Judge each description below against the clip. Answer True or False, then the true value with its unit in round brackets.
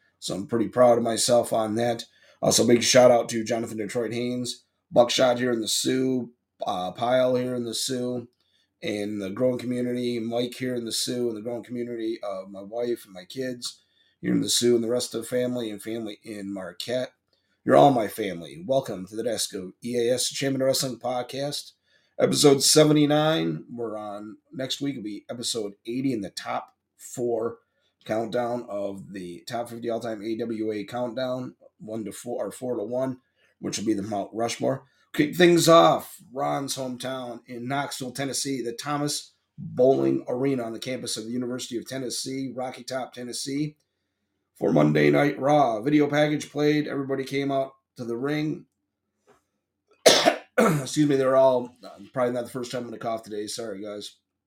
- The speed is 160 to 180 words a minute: True (175 wpm)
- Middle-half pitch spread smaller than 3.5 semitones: True (2.9 semitones)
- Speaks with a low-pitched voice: True (120 Hz)